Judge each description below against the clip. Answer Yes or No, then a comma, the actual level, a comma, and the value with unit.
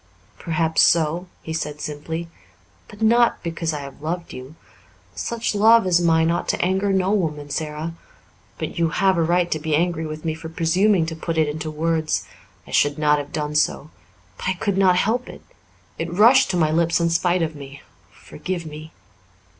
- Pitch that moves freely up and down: No, average, 2.9 semitones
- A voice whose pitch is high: No, medium, 165 Hz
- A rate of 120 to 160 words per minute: No, average, 190 wpm